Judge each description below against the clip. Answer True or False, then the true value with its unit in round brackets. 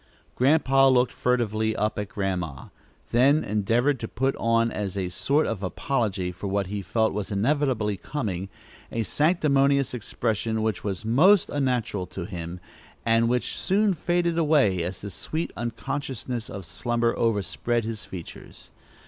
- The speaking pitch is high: False (115 Hz)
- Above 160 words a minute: False (145 wpm)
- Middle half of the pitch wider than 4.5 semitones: True (5.2 semitones)